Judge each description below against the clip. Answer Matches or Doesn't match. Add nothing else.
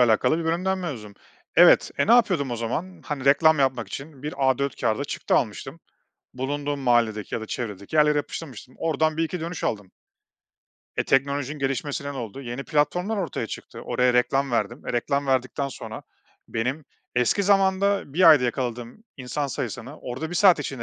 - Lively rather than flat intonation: Doesn't match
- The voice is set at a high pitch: Doesn't match